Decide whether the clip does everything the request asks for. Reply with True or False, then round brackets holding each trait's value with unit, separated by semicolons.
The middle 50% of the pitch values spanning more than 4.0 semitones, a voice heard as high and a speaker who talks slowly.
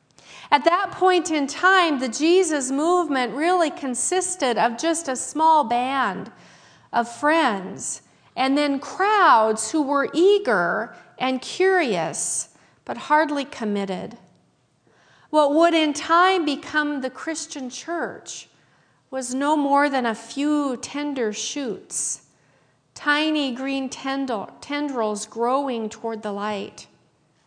True (4.5 semitones; 285 Hz; 110 wpm)